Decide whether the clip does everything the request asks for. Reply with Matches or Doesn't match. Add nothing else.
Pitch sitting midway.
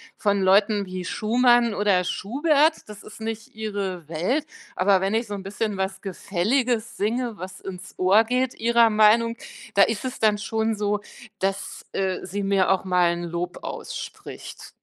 Doesn't match